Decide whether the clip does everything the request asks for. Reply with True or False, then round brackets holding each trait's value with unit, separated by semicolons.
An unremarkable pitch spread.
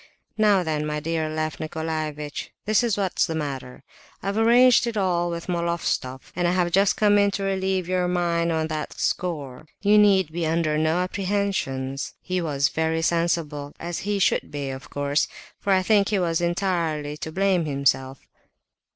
True (3.9 semitones)